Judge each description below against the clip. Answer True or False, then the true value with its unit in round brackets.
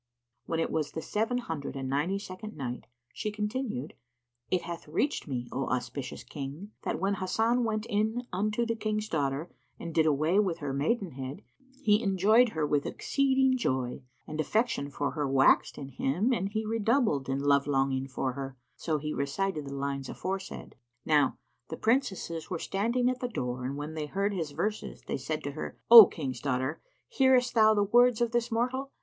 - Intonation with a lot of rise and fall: True (7.7 semitones)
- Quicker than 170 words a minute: True (180 wpm)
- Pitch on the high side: False (170 Hz)